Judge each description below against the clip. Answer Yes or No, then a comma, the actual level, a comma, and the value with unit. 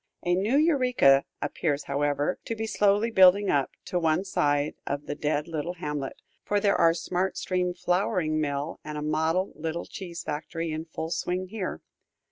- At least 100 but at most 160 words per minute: No, average, 170 wpm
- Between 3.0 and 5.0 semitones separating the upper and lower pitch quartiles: Yes, average, 3.9 semitones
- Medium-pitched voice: Yes, medium, 170 Hz